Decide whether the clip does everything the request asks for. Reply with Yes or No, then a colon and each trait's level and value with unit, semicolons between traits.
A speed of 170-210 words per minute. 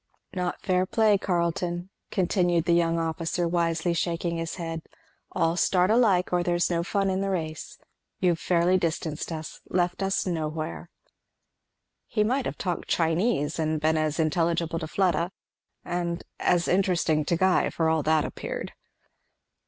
No: average, 150 wpm